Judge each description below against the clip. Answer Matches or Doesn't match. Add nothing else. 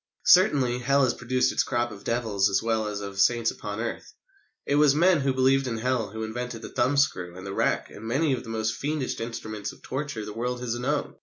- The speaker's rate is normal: Doesn't match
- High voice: Doesn't match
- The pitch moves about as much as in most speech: Matches